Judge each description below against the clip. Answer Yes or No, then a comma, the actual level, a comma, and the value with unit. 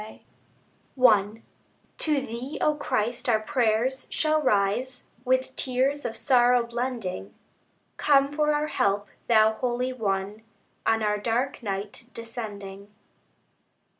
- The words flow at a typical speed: No, slow, 115 wpm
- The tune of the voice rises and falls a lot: No, average, 3.6 semitones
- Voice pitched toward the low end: No, high, 235 Hz